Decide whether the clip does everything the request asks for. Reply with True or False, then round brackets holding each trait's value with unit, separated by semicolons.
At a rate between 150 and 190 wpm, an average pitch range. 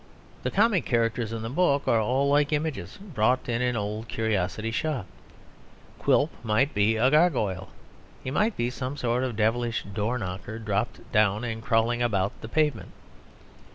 True (160 wpm; 3.9 semitones)